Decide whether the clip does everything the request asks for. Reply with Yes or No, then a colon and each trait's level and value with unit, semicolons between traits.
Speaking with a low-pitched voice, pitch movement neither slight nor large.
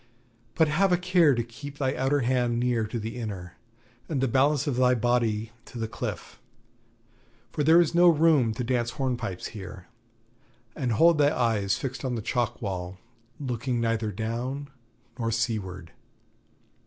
Yes: low, 120 Hz; average, 4.1 semitones